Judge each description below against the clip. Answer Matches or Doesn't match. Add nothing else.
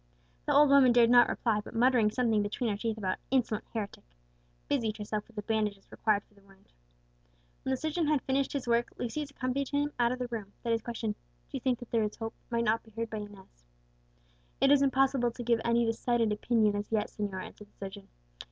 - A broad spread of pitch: Doesn't match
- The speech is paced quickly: Matches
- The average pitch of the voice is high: Matches